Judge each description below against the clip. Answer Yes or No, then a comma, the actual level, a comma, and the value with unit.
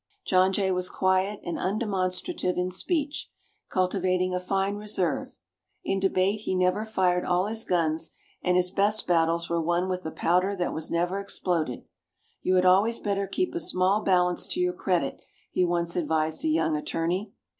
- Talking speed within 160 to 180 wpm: Yes, average, 170 wpm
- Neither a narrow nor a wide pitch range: No, narrow, 2.2 semitones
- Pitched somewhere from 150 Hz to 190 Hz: Yes, medium, 185 Hz